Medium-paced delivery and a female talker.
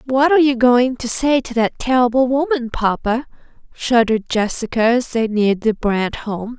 Yes: average, 175 wpm; female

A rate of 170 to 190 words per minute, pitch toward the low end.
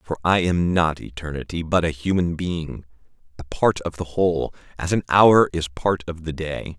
Yes: average, 185 wpm; very low, 85 Hz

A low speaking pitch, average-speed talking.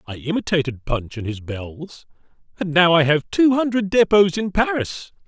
No: medium, 160 Hz; average, 170 wpm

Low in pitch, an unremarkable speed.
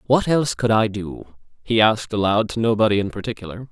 Yes: low, 110 Hz; average, 195 wpm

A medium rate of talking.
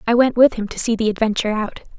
No: fast, 275 wpm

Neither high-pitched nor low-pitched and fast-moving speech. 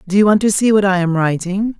No: high, 195 Hz; fast, 300 wpm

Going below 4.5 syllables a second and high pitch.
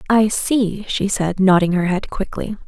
Yes: 4.2 syllables/s; high, 195 Hz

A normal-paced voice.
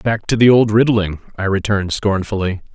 Yes: average, 175 wpm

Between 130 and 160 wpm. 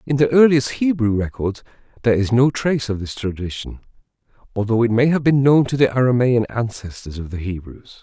No: average, 185 wpm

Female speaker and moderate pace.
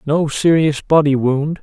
No: male; average, 150 wpm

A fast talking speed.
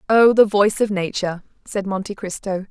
No: average, 180 wpm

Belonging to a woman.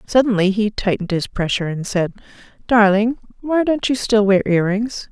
Yes: female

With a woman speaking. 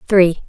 Yes: female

